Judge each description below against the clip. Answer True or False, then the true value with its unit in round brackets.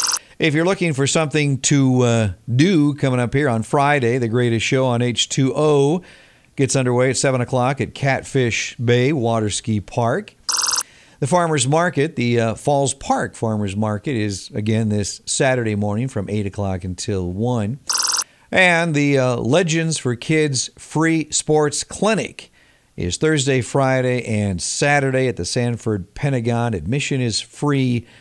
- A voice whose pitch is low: True (125 Hz)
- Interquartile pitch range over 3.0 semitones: True (4.5 semitones)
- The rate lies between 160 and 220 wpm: False (145 wpm)